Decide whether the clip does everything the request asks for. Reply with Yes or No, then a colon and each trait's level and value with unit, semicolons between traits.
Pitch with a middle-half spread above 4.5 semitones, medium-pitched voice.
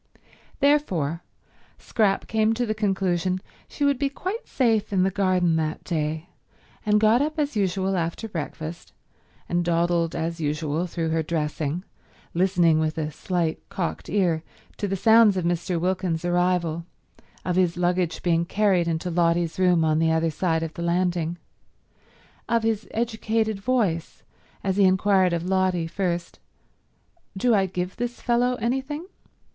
No: average, 4.0 semitones; medium, 180 Hz